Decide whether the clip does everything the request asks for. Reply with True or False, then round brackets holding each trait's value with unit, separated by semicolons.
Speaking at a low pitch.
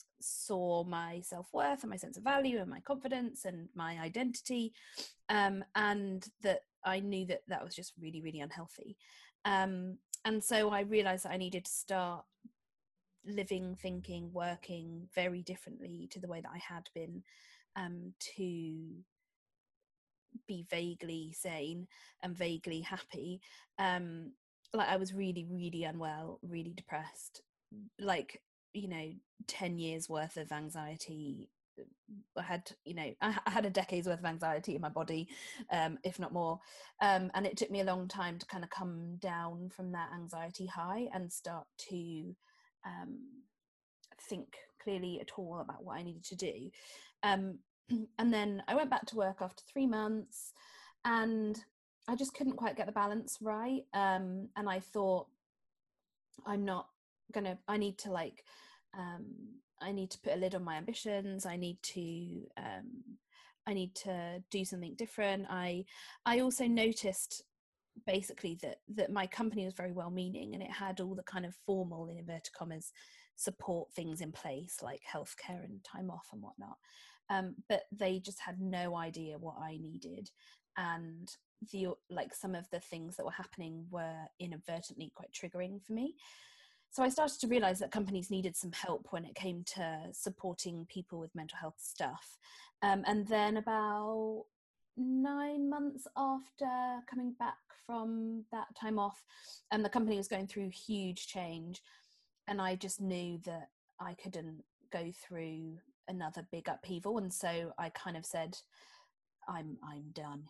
False (190 Hz)